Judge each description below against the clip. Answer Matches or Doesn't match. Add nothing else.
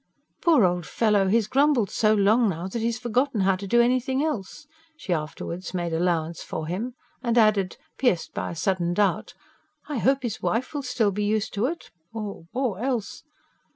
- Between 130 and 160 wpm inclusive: Doesn't match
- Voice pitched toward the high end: Matches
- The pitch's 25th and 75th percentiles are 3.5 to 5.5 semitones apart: Matches